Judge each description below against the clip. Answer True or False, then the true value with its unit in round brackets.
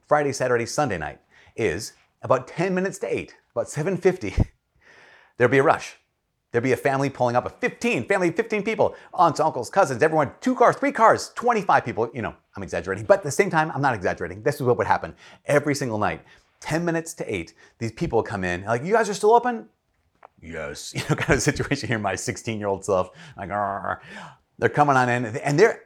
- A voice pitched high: False (150 Hz)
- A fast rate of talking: True (210 wpm)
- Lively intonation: True (7.9 semitones)